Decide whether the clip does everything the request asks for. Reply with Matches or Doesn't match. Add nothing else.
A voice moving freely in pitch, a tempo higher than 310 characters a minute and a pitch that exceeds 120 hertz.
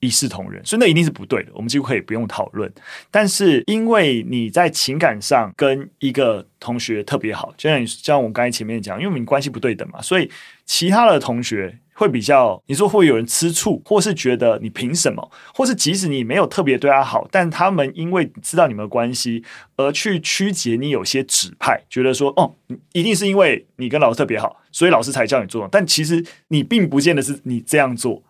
Matches